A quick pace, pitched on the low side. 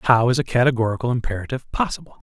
No: average, 160 wpm; low, 125 Hz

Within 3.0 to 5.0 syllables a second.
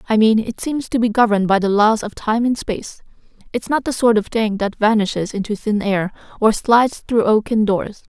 No: 5.4 syllables/s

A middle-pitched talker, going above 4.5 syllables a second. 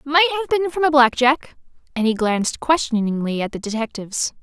No: very high, 265 Hz; 5.9 syllables/s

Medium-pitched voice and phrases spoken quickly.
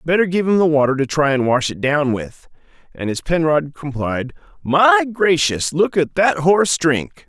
No: medium, 155 Hz; average, 190 wpm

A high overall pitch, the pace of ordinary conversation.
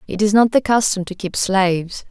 No: high, 200 Hz; fast, 230 wpm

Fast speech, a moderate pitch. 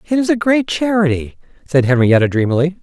No: average, 170 wpm; medium, 170 Hz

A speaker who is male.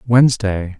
Yes: male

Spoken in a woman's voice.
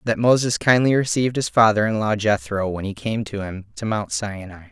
No: male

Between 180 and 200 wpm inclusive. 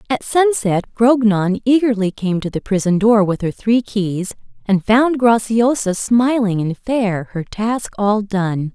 No: average, 160 wpm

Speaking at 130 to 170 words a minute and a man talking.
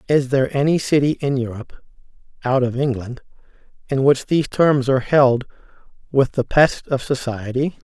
Yes: average, 150 wpm; male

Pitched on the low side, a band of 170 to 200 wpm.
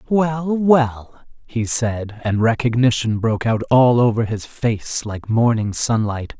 No: low, 120 Hz; average, 140 wpm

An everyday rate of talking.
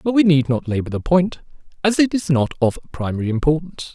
No: fast, 215 wpm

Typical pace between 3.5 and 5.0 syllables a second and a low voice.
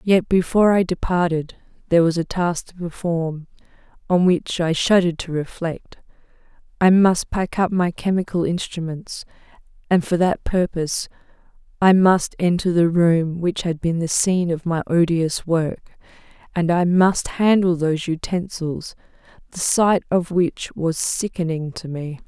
No: 4.5 syllables/s; medium, 170 Hz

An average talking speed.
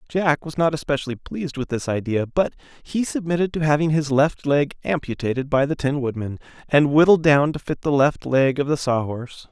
No: fast, 210 wpm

